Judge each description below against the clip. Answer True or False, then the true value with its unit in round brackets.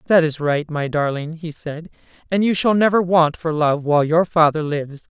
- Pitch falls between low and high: True (160 Hz)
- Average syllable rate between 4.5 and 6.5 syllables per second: True (5.2 syllables/s)